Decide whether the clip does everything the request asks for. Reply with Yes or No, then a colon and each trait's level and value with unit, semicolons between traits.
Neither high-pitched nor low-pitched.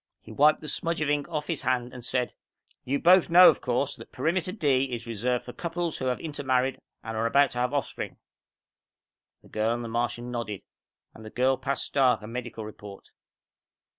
No: low, 130 Hz